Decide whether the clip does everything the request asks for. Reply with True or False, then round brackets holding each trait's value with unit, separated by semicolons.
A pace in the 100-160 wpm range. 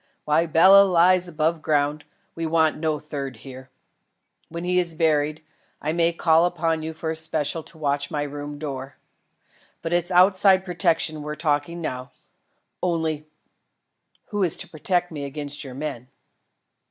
True (155 wpm)